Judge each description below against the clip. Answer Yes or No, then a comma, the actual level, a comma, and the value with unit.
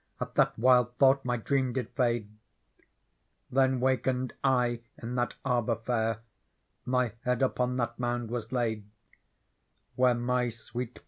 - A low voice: Yes, low, 125 Hz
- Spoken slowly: Yes, slow, 130 wpm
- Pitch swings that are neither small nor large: No, narrow, 1.3 semitones